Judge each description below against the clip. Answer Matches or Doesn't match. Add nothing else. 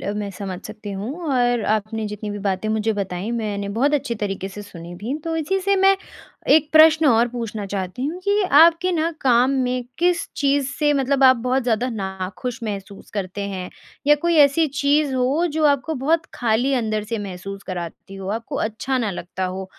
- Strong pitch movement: Matches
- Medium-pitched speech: Doesn't match